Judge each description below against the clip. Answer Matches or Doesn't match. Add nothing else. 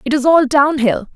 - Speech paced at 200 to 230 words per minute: Doesn't match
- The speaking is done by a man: Doesn't match